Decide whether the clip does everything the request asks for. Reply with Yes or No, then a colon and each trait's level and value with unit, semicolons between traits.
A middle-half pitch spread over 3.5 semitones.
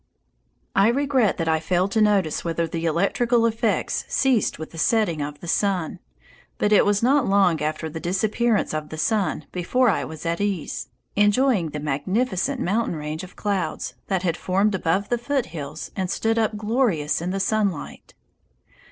Yes: average, 5.1 semitones